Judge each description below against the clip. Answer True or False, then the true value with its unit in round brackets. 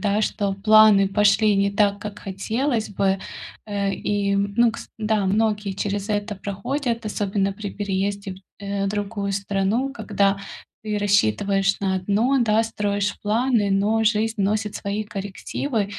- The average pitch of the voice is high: True (205 Hz)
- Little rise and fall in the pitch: True (1.5 semitones)